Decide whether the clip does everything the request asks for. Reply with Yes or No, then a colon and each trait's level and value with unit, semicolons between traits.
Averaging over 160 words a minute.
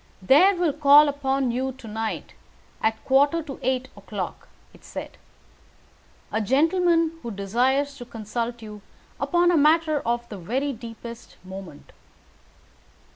No: slow, 135 wpm